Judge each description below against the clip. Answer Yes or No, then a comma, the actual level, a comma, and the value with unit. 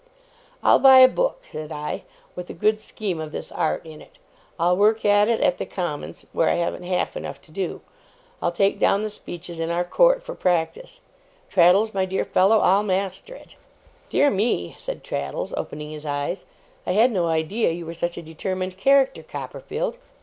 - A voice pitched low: No, medium, 185 Hz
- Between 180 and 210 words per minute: Yes, average, 190 wpm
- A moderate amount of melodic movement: Yes, average, 4.6 semitones